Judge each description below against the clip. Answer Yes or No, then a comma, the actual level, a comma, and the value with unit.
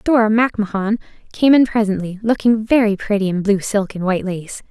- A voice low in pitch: No, high, 210 Hz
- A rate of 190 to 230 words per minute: No, average, 180 wpm